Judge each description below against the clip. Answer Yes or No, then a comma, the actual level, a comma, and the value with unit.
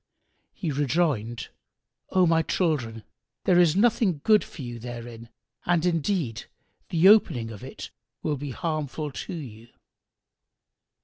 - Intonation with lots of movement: Yes, wide, 6.6 semitones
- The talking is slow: Yes, slow, 125 wpm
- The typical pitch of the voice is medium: Yes, medium, 150 Hz